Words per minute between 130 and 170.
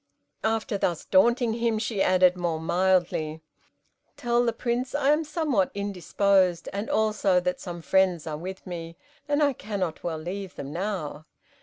Yes: average, 155 wpm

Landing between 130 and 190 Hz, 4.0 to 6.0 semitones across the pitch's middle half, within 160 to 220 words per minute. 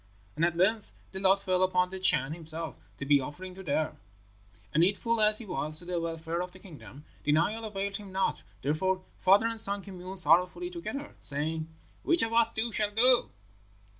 Yes: medium, 185 Hz; average, 4.4 semitones; average, 195 wpm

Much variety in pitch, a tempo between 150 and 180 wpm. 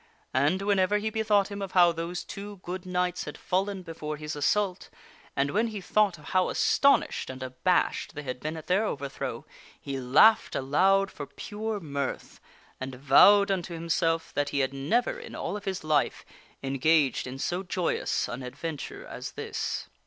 Yes: wide, 5.8 semitones; average, 175 wpm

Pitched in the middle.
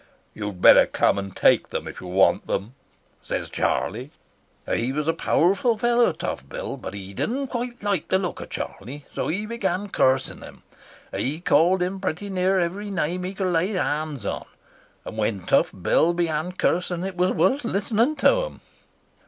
Yes: medium, 180 Hz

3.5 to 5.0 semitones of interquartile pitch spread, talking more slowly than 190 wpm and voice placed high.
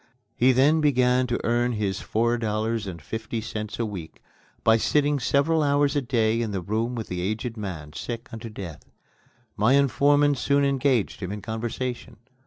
No: average, 3.8 semitones; average, 175 wpm; low, 115 Hz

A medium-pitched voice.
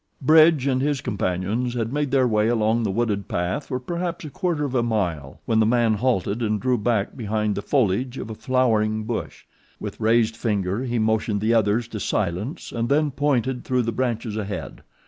No: low, 115 Hz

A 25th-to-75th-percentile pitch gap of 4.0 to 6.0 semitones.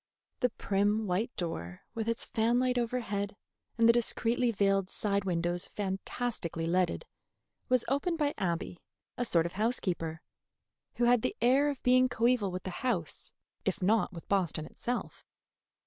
Yes: average, 5.0 semitones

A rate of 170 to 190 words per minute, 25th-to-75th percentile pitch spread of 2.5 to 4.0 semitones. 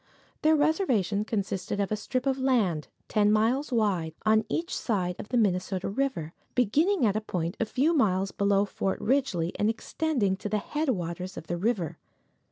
No: average, 175 wpm; wide, 5.6 semitones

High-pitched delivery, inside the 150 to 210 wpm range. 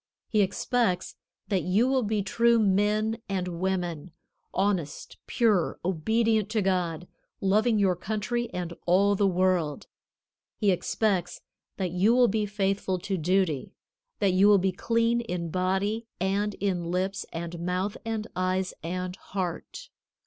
No: high, 195 Hz; average, 140 wpm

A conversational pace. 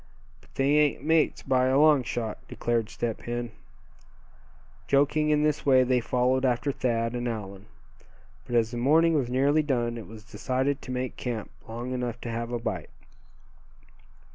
Yes: average, 165 wpm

